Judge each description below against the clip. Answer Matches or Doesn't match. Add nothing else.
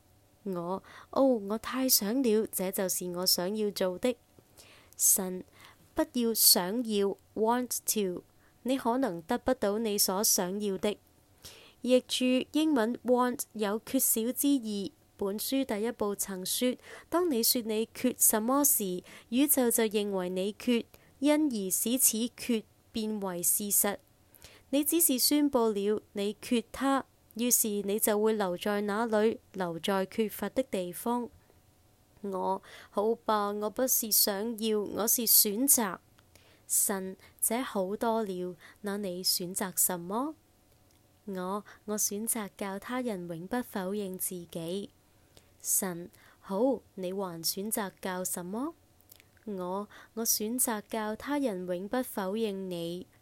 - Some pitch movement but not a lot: Matches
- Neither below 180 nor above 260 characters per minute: Matches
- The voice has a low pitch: Doesn't match